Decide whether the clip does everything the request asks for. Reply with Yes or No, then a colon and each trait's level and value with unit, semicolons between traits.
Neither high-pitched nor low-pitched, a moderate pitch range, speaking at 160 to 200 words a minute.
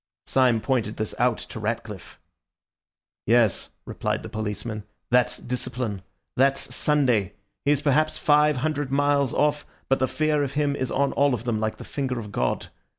No: low, 130 Hz; average, 4.3 semitones; average, 165 wpm